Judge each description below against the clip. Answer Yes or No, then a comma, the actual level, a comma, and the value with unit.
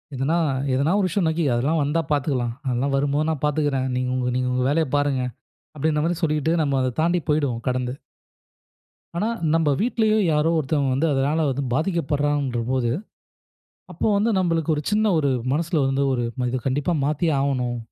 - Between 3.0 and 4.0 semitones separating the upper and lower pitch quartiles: Yes, average, 3.7 semitones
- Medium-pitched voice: Yes, medium, 145 Hz